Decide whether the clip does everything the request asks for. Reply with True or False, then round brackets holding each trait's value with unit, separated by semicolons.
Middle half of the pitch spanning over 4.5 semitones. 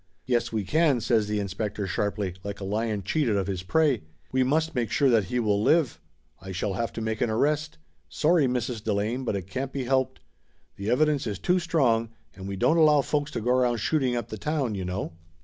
True (5.1 semitones)